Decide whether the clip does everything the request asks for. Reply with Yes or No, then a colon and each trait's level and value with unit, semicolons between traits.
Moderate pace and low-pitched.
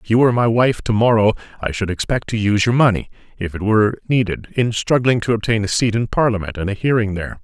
No: fast, 240 wpm; low, 110 Hz